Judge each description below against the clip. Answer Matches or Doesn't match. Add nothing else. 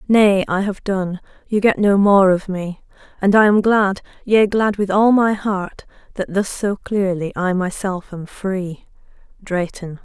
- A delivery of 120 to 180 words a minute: Matches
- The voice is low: Doesn't match